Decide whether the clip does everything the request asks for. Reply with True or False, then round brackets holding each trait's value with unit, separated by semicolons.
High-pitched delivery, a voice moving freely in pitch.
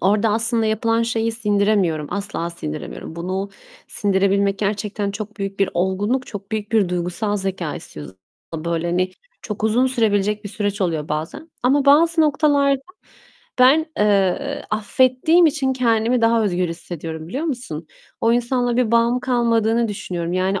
False (210 Hz; 4.2 semitones)